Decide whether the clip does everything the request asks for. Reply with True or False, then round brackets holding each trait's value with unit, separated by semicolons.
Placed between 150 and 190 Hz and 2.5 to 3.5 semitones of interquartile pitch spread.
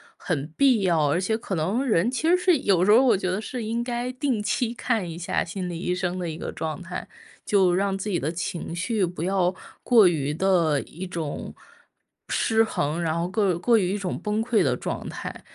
False (185 Hz; 4.6 semitones)